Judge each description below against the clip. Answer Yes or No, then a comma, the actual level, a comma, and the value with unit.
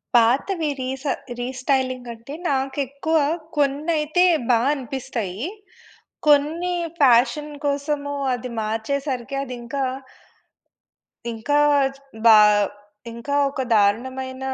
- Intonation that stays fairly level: No, average, 3.0 semitones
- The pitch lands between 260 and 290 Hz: Yes, very high, 265 Hz